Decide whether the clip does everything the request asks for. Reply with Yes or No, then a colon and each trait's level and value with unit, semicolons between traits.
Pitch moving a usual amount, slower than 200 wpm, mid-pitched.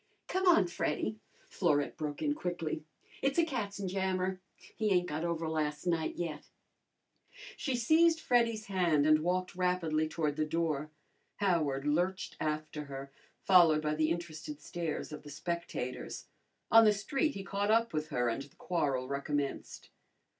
Yes: average, 4.5 semitones; average, 150 wpm; medium, 170 Hz